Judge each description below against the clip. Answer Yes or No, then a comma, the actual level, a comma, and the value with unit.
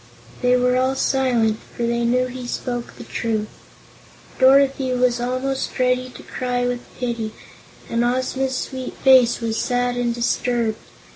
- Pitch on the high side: Yes, high, 245 Hz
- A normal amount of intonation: No, narrow, 1.4 semitones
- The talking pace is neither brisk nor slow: Yes, average, 145 wpm